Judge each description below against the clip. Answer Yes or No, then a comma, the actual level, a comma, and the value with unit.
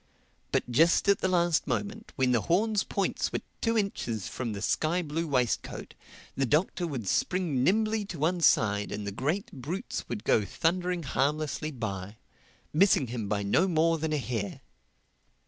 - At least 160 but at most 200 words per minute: Yes, average, 165 wpm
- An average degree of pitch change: No, wide, 7.0 semitones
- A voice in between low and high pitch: Yes, medium, 155 Hz